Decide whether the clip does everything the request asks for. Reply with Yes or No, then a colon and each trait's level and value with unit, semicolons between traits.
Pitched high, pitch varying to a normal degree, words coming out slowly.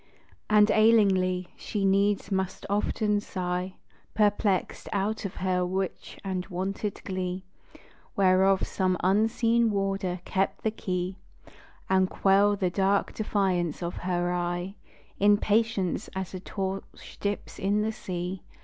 No: high, 195 Hz; narrow, 1.9 semitones; slow, 120 wpm